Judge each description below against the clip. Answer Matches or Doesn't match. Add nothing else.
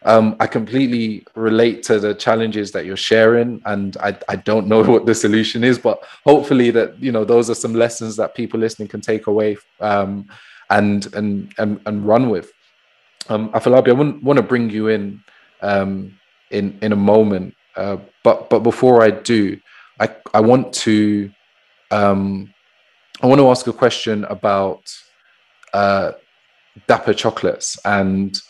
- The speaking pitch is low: Matches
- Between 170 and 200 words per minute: Doesn't match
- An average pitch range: Doesn't match